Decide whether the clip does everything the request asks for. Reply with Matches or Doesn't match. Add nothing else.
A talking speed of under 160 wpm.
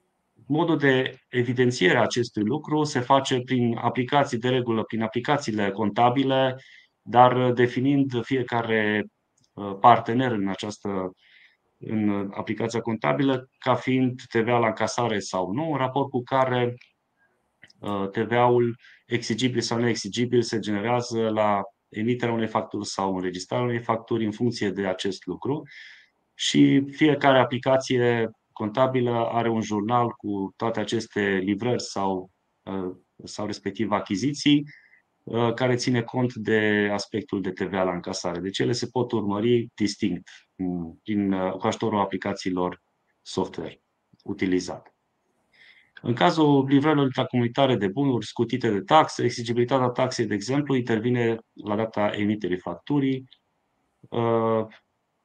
Matches